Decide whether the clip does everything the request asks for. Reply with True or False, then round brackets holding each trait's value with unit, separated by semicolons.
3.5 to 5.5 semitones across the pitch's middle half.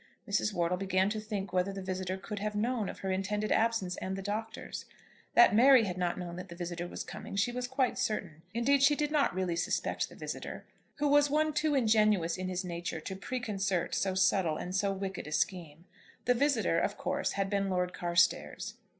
True (3.8 semitones)